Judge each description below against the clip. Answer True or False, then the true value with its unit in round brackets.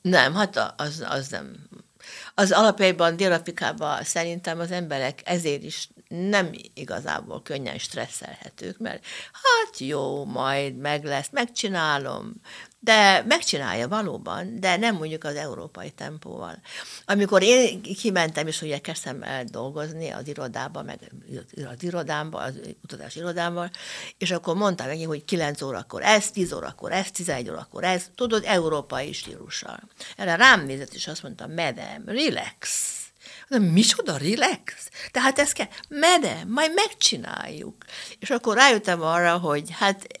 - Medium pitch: True (180 Hz)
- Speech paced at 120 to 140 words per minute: True (135 wpm)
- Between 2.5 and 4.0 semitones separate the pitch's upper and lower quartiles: False (5.5 semitones)